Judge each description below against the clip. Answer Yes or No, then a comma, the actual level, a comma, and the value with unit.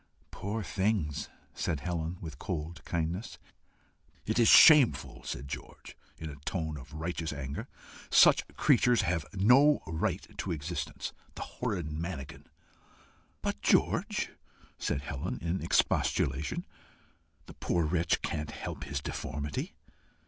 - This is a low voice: Yes, very low, 80 Hz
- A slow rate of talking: Yes, slow, 120 wpm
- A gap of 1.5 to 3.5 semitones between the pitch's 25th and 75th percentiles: No, average, 4.3 semitones